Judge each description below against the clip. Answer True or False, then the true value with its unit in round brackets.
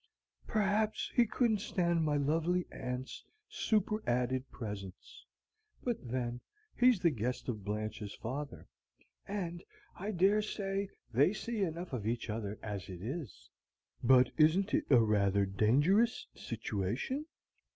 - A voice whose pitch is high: False (140 Hz)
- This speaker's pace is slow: True (125 wpm)